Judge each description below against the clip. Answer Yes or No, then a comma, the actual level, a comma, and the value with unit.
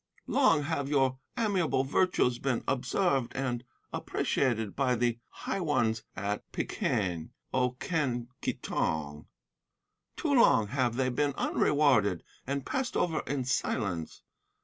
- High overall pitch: No, low, 130 Hz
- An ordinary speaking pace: No, slow, 125 wpm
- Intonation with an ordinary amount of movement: Yes, average, 3.8 semitones